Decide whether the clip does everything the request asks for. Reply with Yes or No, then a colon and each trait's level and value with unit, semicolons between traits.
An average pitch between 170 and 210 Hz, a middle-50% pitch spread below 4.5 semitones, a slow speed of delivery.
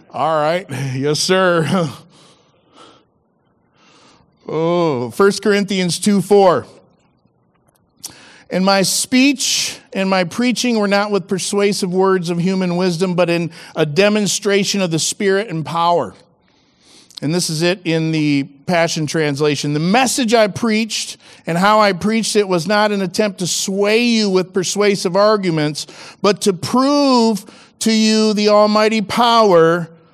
Yes: high, 190 Hz; average, 3.9 semitones; slow, 130 wpm